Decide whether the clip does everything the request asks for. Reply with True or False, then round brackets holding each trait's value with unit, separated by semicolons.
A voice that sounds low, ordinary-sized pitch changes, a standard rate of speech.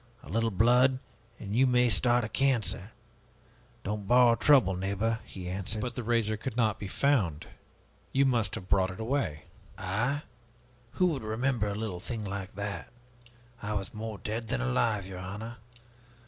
True (110 Hz; 3.8 semitones; 165 wpm)